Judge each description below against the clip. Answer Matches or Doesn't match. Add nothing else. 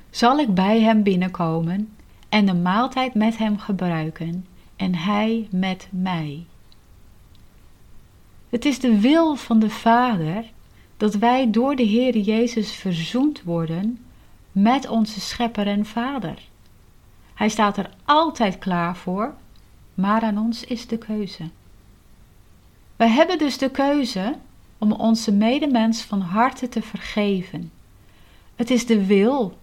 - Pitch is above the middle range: Matches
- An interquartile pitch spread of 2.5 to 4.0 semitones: Doesn't match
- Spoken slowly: Matches